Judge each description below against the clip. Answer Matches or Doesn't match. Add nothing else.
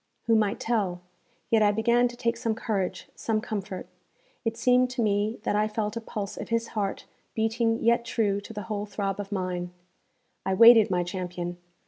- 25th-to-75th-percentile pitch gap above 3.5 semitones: Doesn't match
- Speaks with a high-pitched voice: Matches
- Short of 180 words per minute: Doesn't match